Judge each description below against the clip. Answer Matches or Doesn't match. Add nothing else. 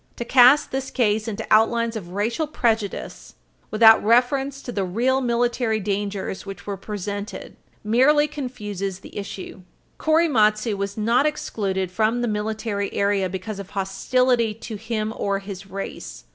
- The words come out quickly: Doesn't match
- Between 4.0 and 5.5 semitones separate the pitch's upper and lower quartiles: Doesn't match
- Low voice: Doesn't match